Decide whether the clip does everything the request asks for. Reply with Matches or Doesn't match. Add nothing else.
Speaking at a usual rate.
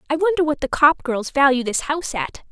Doesn't match